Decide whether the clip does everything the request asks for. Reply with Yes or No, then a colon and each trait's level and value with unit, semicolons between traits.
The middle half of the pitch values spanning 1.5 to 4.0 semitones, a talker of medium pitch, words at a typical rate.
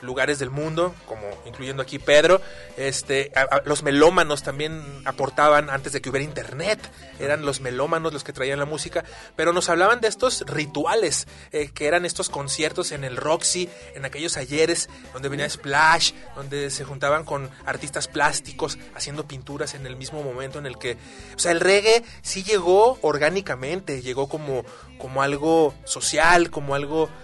Yes: average, 3.1 semitones; medium, 145 Hz; average, 165 wpm